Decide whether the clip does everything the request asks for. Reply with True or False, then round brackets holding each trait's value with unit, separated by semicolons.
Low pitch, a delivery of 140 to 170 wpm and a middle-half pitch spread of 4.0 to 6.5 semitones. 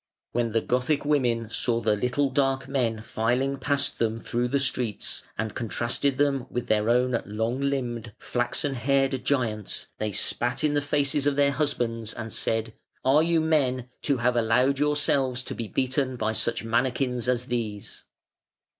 False (125 Hz; 165 wpm; 3.2 semitones)